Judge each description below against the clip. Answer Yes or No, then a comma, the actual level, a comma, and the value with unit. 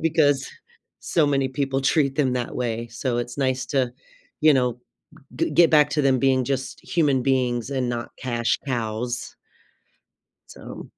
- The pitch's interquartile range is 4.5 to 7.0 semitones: No, narrow, 2.5 semitones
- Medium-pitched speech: No, low, 130 Hz